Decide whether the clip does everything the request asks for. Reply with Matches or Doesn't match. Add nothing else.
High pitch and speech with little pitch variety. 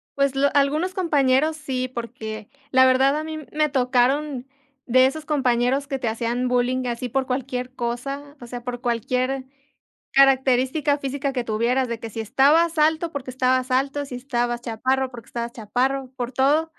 Matches